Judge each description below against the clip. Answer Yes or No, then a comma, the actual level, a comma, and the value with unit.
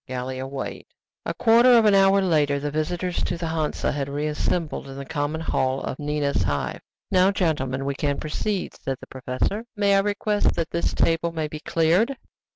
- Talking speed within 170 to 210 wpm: Yes, average, 185 wpm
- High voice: No, medium, 155 Hz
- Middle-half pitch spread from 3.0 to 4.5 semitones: No, average, 5.2 semitones